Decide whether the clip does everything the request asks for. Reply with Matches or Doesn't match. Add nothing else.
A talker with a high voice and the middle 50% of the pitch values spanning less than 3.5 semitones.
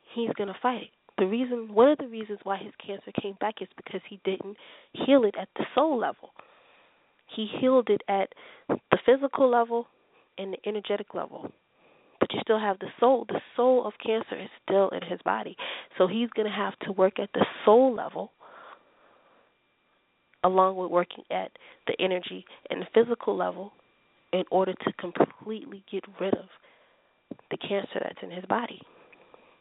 Doesn't match